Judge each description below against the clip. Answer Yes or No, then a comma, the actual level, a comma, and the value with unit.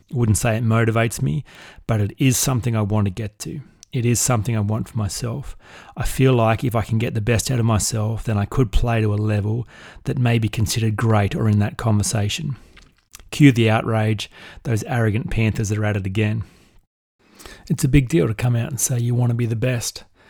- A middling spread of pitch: No, narrow, 2.3 semitones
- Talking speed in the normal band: No, fast, 220 wpm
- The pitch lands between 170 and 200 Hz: No, low, 115 Hz